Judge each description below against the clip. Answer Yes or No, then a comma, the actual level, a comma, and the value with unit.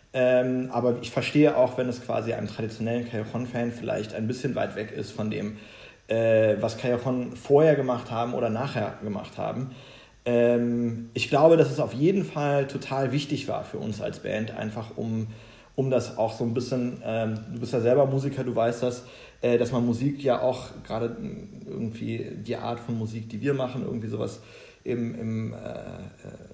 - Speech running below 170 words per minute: No, average, 185 wpm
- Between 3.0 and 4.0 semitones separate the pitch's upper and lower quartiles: No, narrow, 2.4 semitones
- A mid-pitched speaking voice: No, low, 120 Hz